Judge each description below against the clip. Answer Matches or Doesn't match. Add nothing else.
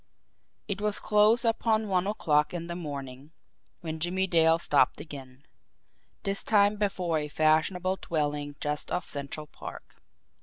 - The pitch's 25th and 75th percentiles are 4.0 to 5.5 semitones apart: Matches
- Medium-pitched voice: Matches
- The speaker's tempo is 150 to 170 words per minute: Doesn't match